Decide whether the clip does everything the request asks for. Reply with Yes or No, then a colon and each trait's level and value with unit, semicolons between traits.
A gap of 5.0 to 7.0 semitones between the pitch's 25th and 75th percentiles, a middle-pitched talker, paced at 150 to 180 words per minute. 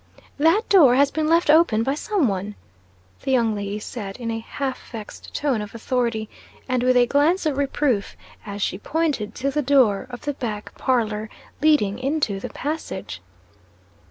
No: wide, 5.4 semitones; very high, 255 Hz; average, 170 wpm